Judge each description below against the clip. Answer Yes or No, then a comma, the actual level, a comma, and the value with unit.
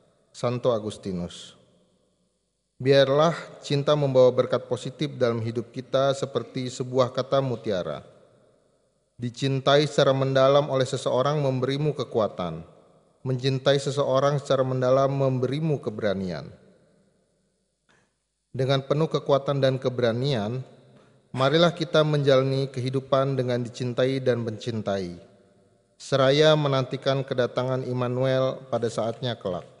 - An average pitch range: No, narrow, 2.2 semitones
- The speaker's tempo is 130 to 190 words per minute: No, average, 95 wpm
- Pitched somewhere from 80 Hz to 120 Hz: No, low, 130 Hz